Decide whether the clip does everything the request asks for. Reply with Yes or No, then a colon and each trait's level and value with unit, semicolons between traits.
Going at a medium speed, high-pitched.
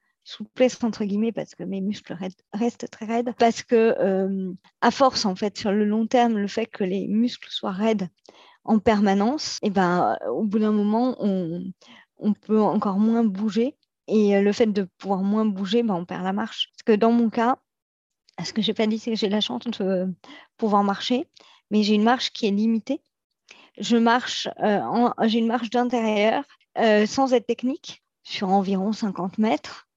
Yes: average, 200 wpm; high, 220 Hz